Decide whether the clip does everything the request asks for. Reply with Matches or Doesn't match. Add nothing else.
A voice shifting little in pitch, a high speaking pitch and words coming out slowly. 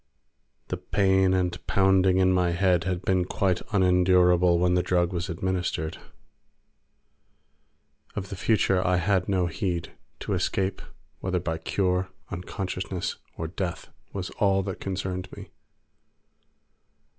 Doesn't match